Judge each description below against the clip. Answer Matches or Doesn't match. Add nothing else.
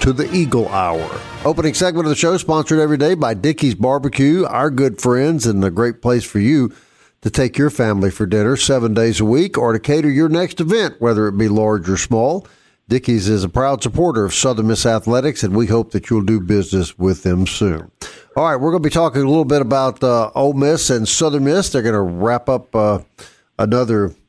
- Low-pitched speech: Matches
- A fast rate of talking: Matches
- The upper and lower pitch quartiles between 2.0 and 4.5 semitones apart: Doesn't match